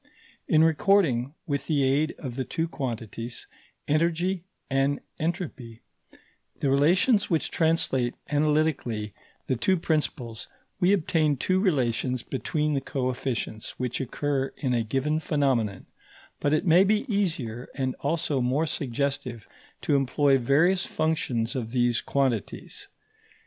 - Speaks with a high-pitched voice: No, medium, 140 Hz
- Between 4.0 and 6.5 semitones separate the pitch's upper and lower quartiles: Yes, average, 4.3 semitones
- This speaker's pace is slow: Yes, slow, 125 wpm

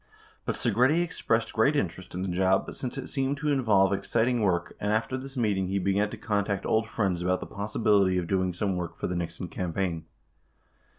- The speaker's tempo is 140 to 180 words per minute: No, average, 200 wpm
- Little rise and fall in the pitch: No, average, 4.0 semitones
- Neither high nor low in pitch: No, low, 100 Hz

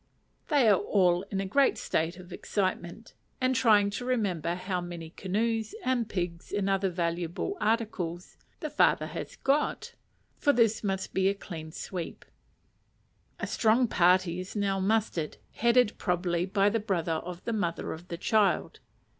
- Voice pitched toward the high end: Yes, high, 195 Hz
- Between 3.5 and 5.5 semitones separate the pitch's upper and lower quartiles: Yes, average, 4.1 semitones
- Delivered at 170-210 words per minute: No, average, 155 wpm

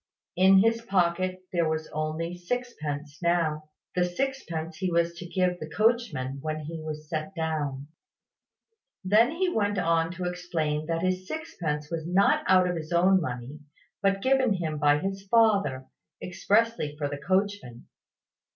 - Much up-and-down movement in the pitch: No, average, 3.9 semitones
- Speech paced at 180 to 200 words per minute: No, average, 150 wpm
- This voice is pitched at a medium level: Yes, medium, 175 Hz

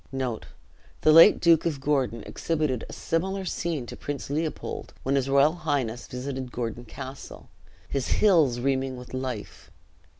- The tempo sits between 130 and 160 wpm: Yes, average, 140 wpm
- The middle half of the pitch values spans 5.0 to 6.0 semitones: No, average, 3.7 semitones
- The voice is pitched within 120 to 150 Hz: Yes, medium, 140 Hz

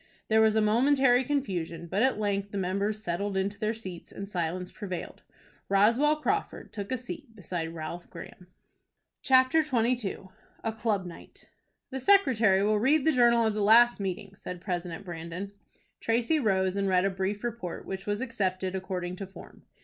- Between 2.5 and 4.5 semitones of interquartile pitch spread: Yes, average, 4.0 semitones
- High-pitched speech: Yes, high, 205 Hz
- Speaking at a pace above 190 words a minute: No, average, 170 wpm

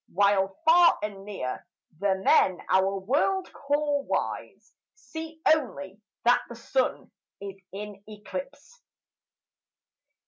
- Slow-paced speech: Yes, slow, 105 wpm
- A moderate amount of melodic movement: No, wide, 7.6 semitones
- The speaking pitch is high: Yes, high, 210 Hz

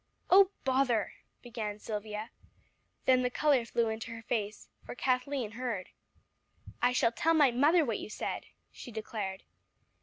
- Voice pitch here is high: Yes, high, 235 Hz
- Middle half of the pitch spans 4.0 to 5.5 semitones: No, average, 3.2 semitones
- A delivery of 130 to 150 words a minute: Yes, average, 145 wpm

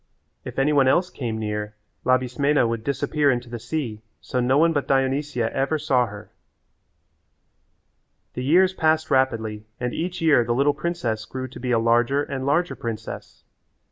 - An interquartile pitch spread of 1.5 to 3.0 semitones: No, average, 3.8 semitones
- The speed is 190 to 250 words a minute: No, average, 165 wpm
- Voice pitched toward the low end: Yes, low, 130 Hz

